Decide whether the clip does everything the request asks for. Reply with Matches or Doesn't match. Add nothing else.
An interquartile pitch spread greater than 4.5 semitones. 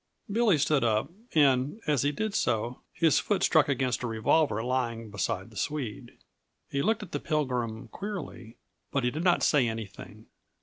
Matches